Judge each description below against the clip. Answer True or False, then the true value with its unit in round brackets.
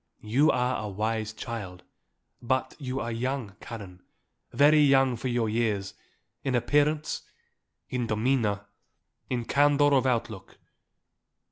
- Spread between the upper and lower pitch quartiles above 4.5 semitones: False (3.8 semitones)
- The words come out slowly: True (120 wpm)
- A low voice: True (120 Hz)